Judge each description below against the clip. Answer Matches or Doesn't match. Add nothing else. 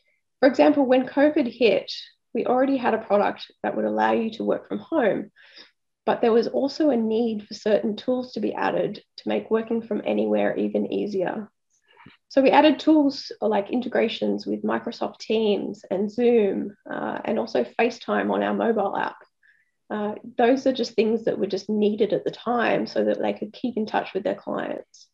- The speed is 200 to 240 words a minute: Doesn't match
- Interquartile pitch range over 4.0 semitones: Matches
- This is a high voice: Matches